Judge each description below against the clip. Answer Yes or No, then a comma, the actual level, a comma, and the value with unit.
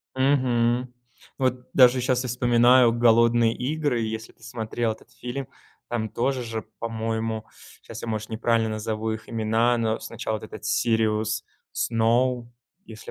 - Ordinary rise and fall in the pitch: No, narrow, 1.7 semitones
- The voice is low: Yes, low, 115 Hz